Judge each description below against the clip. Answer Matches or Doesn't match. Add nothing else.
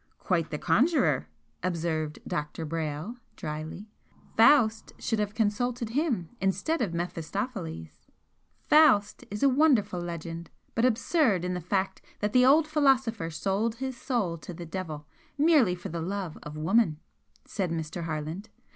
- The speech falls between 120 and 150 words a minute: Matches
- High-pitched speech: Matches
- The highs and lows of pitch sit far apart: Matches